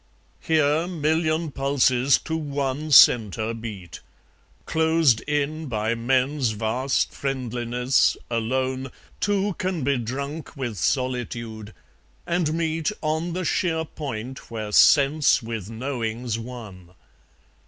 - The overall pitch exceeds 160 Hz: No, low, 130 Hz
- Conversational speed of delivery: No, slow, 105 wpm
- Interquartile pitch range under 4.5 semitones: No, average, 5.1 semitones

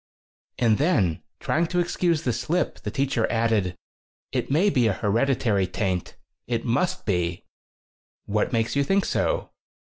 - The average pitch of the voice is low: Yes, low, 120 Hz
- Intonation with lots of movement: Yes, wide, 7.0 semitones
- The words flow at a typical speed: Yes, average, 145 wpm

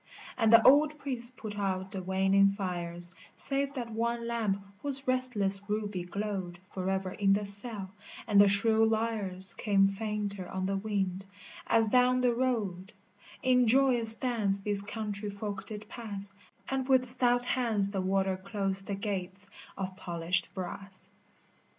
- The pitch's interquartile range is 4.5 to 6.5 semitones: No, average, 3.3 semitones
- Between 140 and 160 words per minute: Yes, average, 150 wpm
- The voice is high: Yes, high, 205 Hz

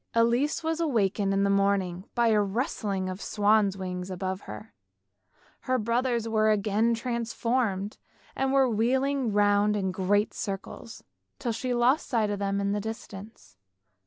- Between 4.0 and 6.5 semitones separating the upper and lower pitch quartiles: No, average, 3.1 semitones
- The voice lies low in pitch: No, high, 210 Hz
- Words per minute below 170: Yes, average, 155 wpm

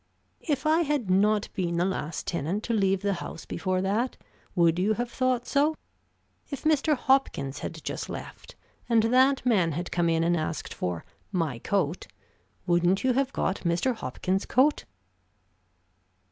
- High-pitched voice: Yes, high, 195 Hz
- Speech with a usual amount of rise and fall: No, wide, 7.0 semitones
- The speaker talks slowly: No, average, 160 wpm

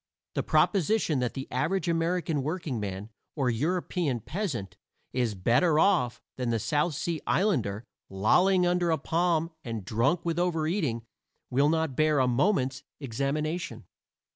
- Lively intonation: Yes, wide, 5.9 semitones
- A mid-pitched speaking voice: Yes, medium, 150 Hz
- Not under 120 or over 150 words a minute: Yes, average, 140 wpm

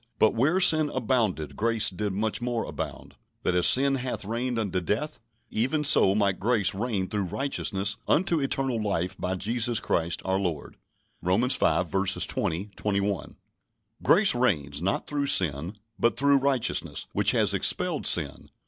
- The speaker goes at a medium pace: Yes, average, 150 wpm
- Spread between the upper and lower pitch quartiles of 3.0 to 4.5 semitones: No, average, 5.3 semitones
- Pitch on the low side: Yes, low, 110 Hz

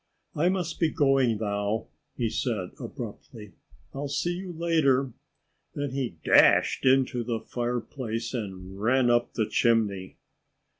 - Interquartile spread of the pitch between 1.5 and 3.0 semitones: No, average, 4.0 semitones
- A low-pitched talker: Yes, low, 120 Hz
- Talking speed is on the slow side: Yes, slow, 130 wpm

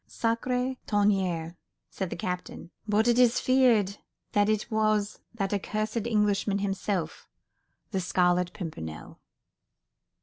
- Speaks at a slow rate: Yes, slow, 105 wpm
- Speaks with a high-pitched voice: Yes, high, 205 Hz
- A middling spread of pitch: Yes, average, 3.3 semitones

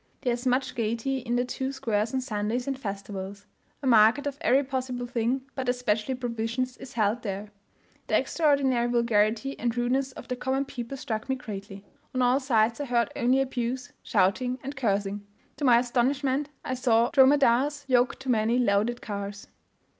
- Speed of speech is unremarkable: Yes, average, 170 wpm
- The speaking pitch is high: Yes, high, 245 Hz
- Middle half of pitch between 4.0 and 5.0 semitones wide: No, average, 3.0 semitones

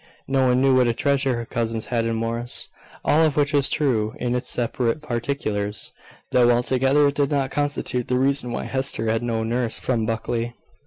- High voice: No, low, 125 Hz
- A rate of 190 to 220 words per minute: Yes, average, 195 wpm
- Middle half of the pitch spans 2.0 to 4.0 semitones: Yes, average, 2.9 semitones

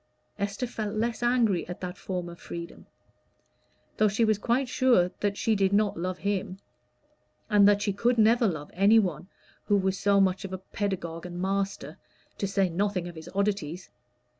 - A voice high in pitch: Yes, high, 200 Hz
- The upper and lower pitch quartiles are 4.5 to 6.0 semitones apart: No, average, 2.7 semitones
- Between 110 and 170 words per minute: No, average, 180 wpm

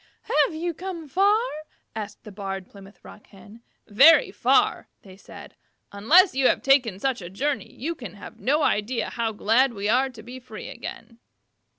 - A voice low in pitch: No, high, 240 Hz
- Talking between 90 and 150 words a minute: No, average, 175 wpm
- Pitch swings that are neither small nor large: No, wide, 6.1 semitones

